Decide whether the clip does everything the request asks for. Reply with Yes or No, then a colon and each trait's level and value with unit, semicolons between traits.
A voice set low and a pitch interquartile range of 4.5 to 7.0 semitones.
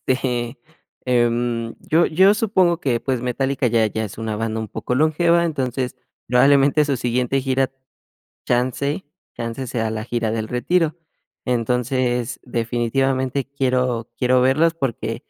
No: low, 125 Hz; average, 2.7 semitones